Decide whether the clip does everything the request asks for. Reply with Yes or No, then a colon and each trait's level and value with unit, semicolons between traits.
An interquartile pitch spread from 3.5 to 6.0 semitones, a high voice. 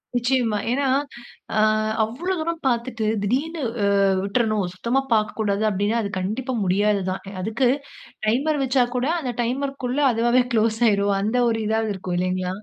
Yes: average, 4.0 semitones; high, 225 Hz